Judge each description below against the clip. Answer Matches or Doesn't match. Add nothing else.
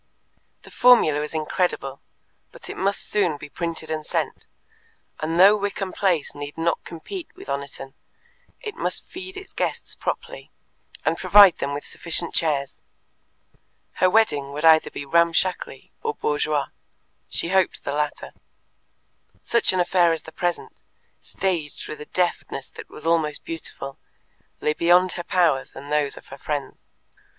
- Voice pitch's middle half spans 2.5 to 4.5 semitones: Matches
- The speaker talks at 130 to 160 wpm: Matches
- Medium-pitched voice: Matches